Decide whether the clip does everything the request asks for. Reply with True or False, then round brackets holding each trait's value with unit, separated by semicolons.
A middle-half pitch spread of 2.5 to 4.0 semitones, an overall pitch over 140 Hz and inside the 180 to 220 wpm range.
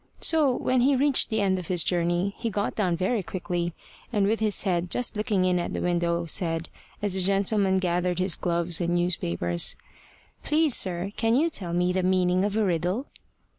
True (3.4 semitones; 185 Hz; 195 wpm)